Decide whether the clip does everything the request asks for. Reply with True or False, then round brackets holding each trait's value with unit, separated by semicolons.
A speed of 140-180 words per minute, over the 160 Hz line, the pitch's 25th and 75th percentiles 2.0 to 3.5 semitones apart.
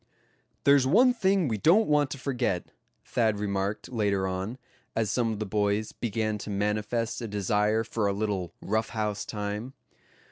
False (165 wpm; 110 Hz; 3.0 semitones)